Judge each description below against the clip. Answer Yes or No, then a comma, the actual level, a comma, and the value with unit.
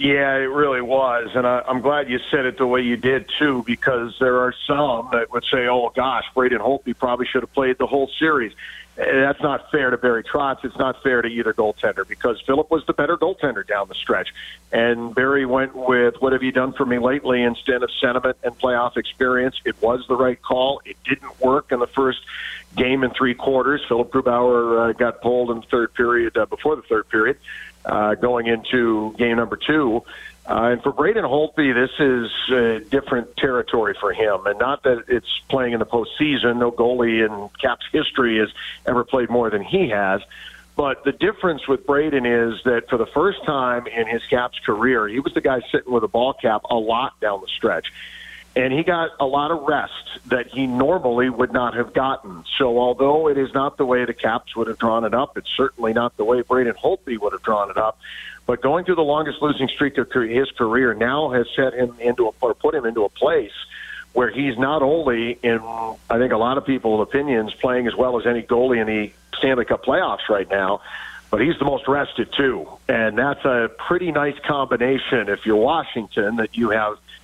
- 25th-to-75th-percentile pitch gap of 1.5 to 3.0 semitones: Yes, narrow, 2.4 semitones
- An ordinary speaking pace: No, fast, 215 wpm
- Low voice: Yes, low, 125 Hz